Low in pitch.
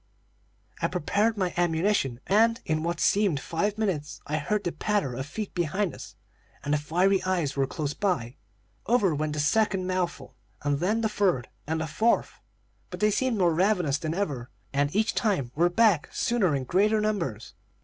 No: medium, 175 Hz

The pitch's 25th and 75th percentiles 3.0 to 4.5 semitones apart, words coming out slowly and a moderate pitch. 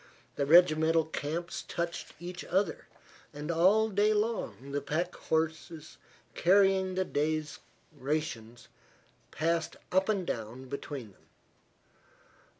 Yes: average, 3.9 semitones; slow, 110 wpm; medium, 165 Hz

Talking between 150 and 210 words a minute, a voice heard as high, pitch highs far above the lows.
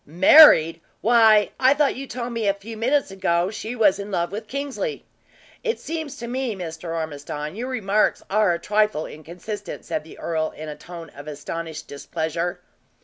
Yes: average, 175 wpm; high, 200 Hz; wide, 6.2 semitones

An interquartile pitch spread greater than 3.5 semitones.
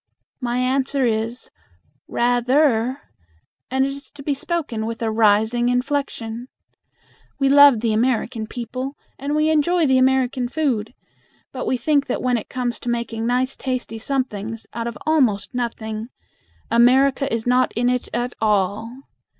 No: average, 3.0 semitones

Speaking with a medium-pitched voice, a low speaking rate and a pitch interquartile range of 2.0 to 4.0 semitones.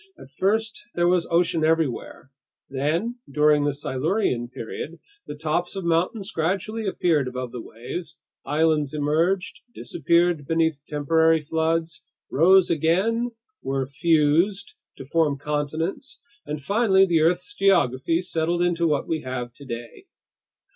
Yes: medium, 160 Hz; slow, 125 wpm; average, 3.3 semitones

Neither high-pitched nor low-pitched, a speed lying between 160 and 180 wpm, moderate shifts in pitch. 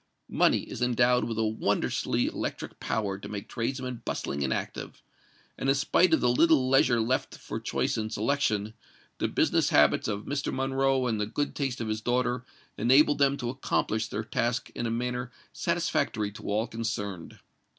No: low, 120 Hz; average, 175 wpm; average, 3.3 semitones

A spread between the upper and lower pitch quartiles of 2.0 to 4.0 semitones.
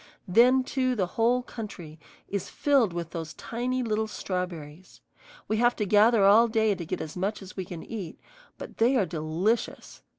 No: average, 4.7 semitones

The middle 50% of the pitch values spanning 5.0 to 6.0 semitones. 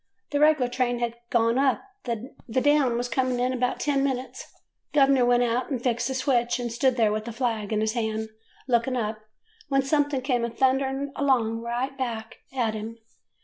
No: narrow, 2.4 semitones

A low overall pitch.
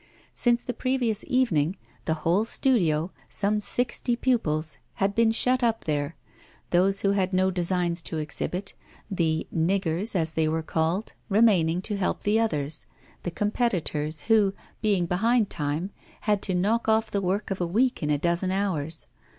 No: high, 190 Hz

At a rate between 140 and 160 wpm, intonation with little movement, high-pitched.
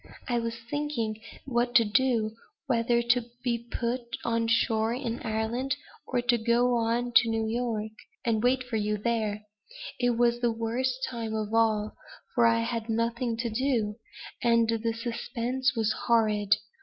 Yes: average, 155 wpm; narrow, 1.4 semitones; high, 230 Hz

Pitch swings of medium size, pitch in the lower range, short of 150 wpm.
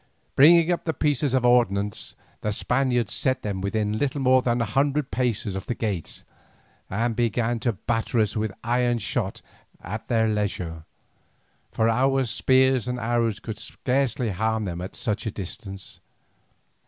No: average, 3.4 semitones; low, 115 Hz; average, 155 wpm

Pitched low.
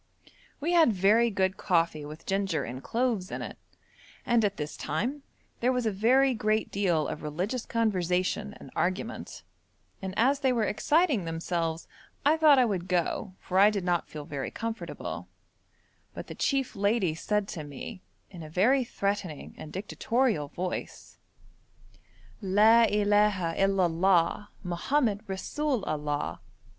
No: high, 200 Hz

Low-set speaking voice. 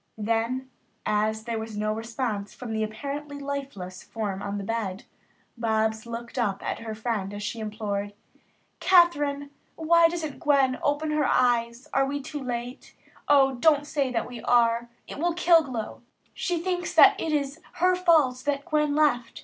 No: very high, 250 Hz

